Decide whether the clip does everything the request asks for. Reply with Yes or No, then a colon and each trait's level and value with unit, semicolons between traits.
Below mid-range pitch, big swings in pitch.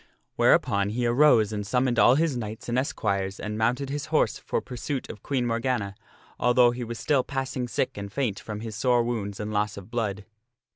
No: low, 120 Hz; average, 3.3 semitones